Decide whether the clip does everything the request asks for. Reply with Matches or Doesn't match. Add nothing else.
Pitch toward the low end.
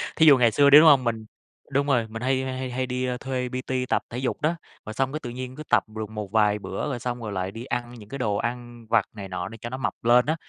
Matches